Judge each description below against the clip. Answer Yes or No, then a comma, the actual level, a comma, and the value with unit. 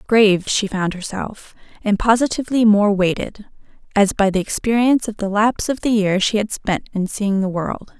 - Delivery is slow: No, average, 190 wpm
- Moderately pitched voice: No, high, 210 Hz